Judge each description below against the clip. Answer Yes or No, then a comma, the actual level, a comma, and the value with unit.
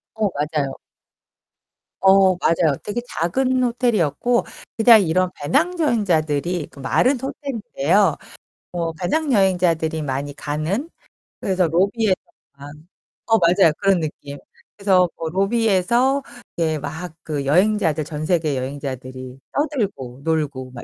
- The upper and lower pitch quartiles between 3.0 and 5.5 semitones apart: No, wide, 6.1 semitones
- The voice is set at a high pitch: No, medium, 175 Hz